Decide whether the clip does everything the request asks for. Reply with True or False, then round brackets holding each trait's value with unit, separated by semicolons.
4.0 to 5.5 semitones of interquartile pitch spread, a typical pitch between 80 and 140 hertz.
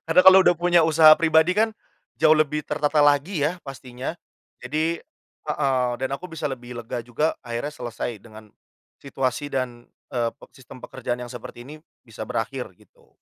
True (4.3 semitones; 135 Hz)